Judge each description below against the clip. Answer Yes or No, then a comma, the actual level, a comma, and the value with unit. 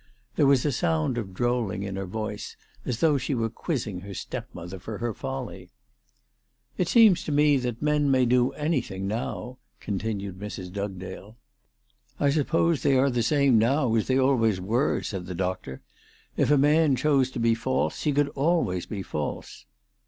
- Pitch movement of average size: No, wide, 6.3 semitones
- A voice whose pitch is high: No, low, 120 Hz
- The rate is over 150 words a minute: Yes, average, 180 wpm